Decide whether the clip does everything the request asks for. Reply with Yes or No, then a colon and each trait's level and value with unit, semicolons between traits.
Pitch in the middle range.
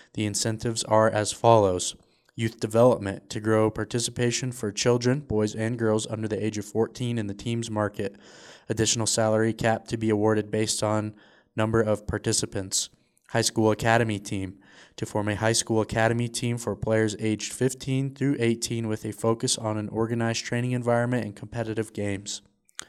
No: low, 110 Hz